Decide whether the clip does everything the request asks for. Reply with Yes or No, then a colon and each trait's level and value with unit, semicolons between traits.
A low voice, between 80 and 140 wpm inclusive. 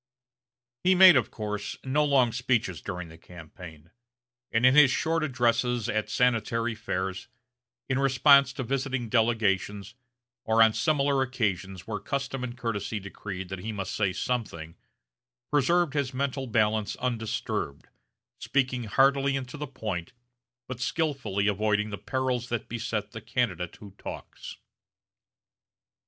Yes: low, 115 Hz; slow, 135 wpm